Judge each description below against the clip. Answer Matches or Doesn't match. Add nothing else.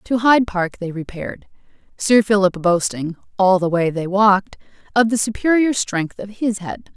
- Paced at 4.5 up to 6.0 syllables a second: Matches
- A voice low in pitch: Doesn't match